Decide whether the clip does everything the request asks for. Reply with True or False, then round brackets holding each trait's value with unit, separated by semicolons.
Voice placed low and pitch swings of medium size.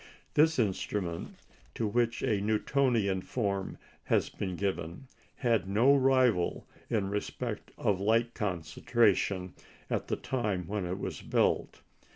True (105 Hz; 3.9 semitones)